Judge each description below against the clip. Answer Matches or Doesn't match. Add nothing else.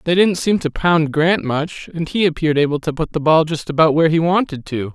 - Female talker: Doesn't match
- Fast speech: Matches